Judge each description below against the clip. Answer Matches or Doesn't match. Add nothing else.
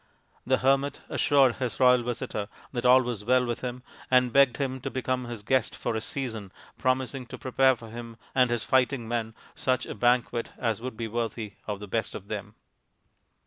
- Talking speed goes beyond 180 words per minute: Matches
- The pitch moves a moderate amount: Doesn't match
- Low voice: Matches